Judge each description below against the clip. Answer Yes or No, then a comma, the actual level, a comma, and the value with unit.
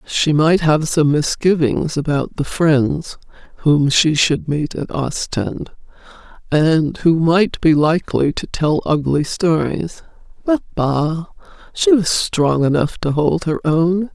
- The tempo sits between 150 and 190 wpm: No, slow, 135 wpm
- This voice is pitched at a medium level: Yes, medium, 155 Hz